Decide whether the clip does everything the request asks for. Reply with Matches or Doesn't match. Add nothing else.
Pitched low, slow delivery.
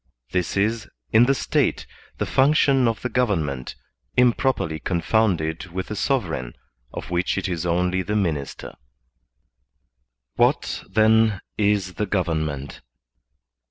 Matches